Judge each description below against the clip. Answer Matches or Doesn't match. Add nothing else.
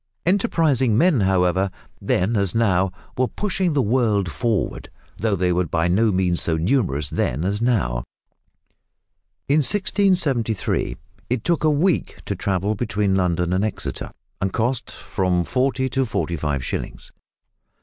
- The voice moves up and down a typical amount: Doesn't match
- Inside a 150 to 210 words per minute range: Doesn't match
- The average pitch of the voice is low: Matches